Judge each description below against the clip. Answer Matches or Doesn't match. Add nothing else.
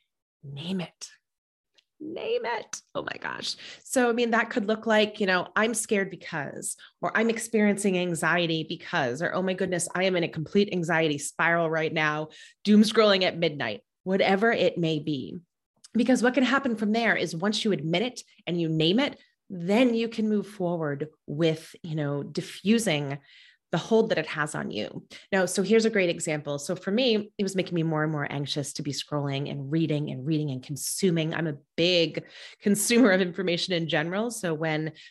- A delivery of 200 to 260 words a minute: Doesn't match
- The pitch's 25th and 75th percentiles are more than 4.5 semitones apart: Matches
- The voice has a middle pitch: Matches